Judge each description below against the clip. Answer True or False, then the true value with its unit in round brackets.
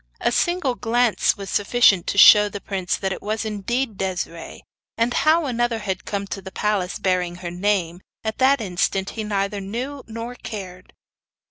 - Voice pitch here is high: True (205 Hz)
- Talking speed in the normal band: True (170 wpm)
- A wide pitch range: False (3.8 semitones)